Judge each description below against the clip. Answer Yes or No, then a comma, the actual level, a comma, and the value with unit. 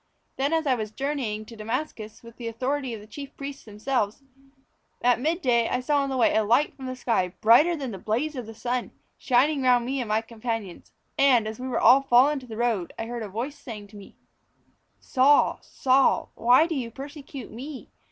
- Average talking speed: No, fast, 220 wpm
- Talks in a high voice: Yes, high, 245 Hz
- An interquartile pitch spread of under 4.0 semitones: Yes, average, 3.6 semitones